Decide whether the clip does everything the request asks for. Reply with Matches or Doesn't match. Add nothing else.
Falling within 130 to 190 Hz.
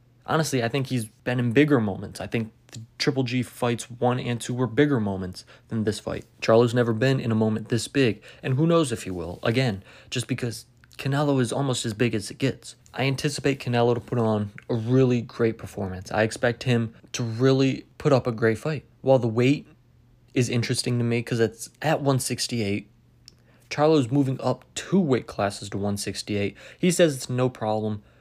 Doesn't match